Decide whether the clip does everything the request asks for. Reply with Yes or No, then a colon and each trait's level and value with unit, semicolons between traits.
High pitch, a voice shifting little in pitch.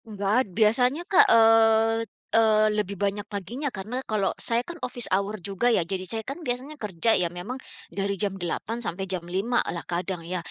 No: high, 215 Hz; average, 3.2 semitones